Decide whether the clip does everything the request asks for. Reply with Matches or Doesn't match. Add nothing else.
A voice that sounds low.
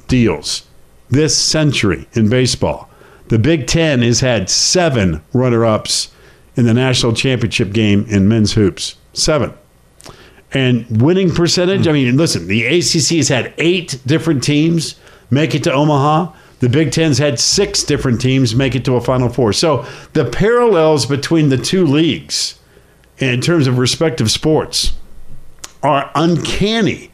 Matches